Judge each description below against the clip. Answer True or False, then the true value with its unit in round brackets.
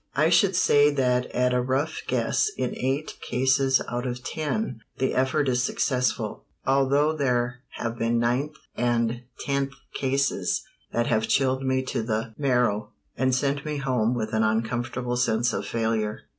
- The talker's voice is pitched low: True (125 Hz)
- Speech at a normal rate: True (155 wpm)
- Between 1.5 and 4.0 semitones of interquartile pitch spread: True (2.5 semitones)